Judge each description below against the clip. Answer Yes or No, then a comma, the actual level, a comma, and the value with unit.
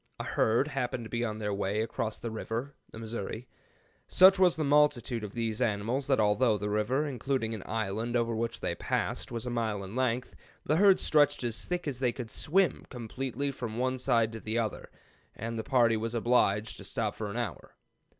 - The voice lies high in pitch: No, low, 115 Hz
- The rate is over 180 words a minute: Yes, fast, 205 wpm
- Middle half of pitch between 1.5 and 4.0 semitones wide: Yes, average, 3.0 semitones